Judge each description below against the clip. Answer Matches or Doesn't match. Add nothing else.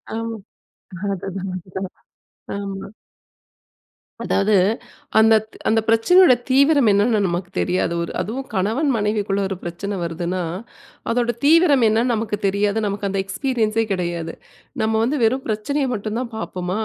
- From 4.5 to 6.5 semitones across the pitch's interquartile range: Doesn't match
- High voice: Matches